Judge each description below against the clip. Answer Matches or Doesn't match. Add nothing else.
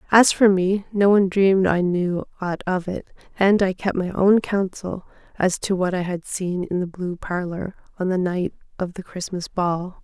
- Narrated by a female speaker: Matches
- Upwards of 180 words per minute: Matches